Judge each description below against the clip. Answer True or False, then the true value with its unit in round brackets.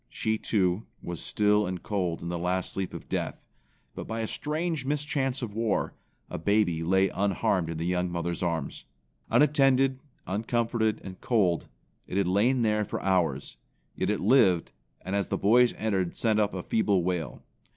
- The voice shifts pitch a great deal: False (4.3 semitones)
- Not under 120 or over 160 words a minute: False (170 wpm)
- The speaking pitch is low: True (100 Hz)